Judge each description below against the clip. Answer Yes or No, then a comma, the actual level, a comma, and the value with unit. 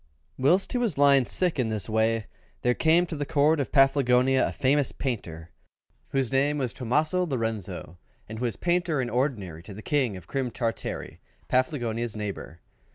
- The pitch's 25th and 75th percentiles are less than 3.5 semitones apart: No, average, 4.5 semitones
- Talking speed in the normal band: Yes, average, 170 wpm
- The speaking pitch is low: Yes, low, 130 Hz